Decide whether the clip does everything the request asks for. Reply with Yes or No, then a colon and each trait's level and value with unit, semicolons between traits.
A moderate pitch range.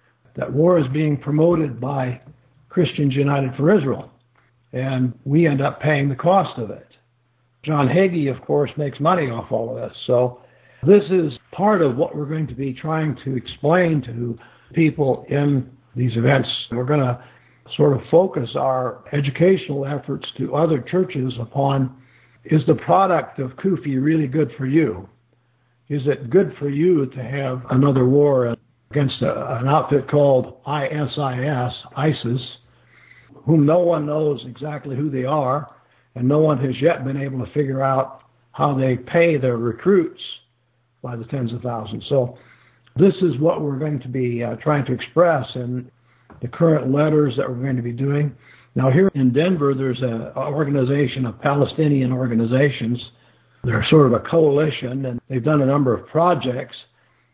Yes: average, 3.3 semitones